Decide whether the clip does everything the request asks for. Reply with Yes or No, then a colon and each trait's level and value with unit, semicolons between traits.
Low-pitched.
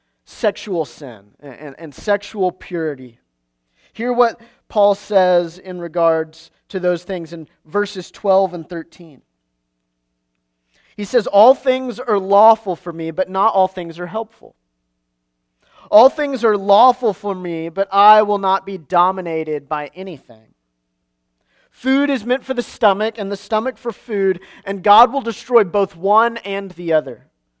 No: medium, 185 Hz